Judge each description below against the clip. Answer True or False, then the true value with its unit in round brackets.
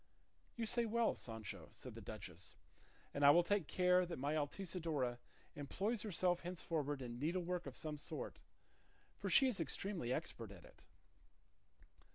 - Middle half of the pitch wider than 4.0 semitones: True (4.8 semitones)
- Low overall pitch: False (165 Hz)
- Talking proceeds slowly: False (150 wpm)